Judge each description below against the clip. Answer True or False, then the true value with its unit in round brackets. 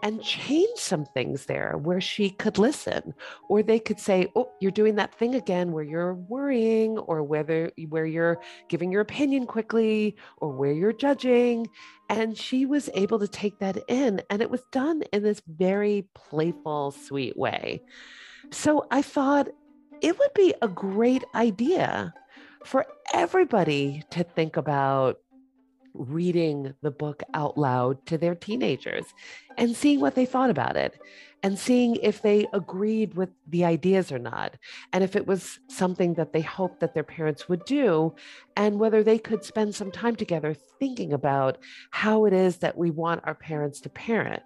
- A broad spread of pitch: True (6.5 semitones)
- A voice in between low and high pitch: False (205 Hz)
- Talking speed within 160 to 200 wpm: True (165 wpm)